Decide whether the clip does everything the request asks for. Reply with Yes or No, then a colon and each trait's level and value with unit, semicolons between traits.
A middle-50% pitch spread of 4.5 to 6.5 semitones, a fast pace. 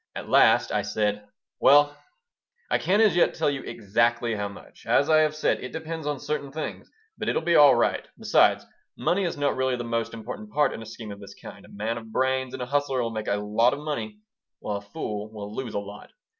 Yes: wide, 5.4 semitones; fast, 230 wpm